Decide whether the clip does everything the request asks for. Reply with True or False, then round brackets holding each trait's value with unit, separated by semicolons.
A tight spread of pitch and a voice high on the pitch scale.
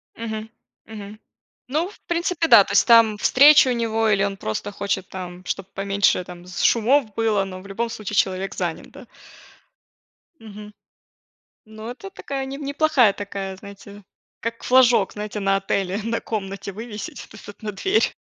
False (3.2 semitones; 210 Hz)